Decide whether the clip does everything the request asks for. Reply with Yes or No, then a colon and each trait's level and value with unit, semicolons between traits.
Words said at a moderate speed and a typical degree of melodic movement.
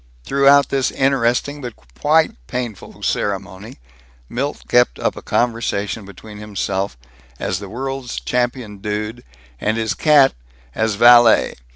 No: slow, 120 wpm; average, 4.3 semitones